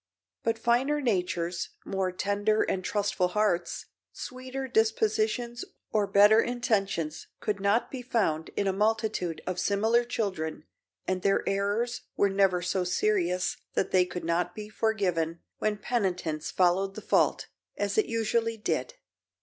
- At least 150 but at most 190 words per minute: No, average, 140 wpm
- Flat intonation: No, average, 3.8 semitones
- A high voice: Yes, high, 205 Hz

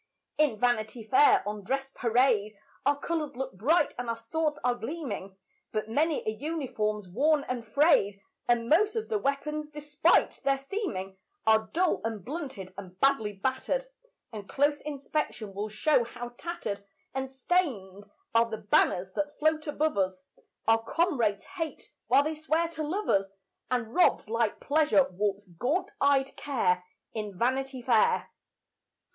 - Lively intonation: Yes, wide, 6.2 semitones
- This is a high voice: Yes, very high, 260 Hz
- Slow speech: No, average, 150 wpm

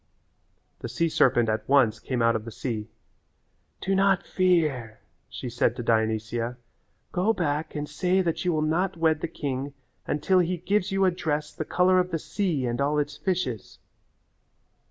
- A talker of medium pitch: Yes, medium, 150 Hz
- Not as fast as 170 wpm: No, average, 175 wpm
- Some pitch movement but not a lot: No, wide, 6.9 semitones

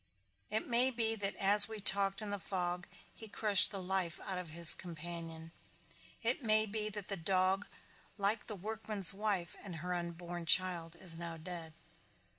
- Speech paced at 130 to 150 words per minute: No, average, 170 wpm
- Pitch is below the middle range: No, high, 190 Hz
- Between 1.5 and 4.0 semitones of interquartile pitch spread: Yes, average, 3.5 semitones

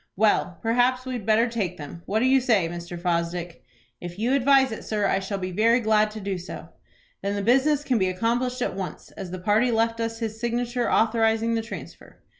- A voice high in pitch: Yes, high, 220 Hz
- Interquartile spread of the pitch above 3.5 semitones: Yes, average, 4.1 semitones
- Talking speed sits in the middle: No, fast, 215 wpm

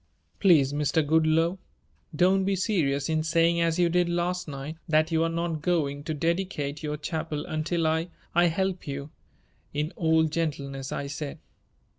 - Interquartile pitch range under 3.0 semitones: Yes, narrow, 2.6 semitones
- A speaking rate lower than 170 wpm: Yes, average, 160 wpm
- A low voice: No, medium, 160 Hz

